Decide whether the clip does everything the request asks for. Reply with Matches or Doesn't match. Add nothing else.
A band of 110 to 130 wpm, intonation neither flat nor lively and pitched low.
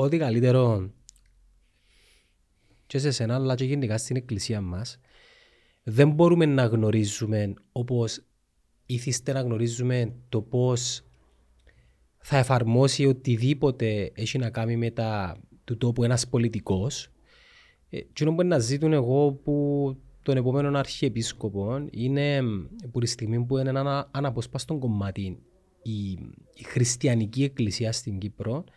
Matches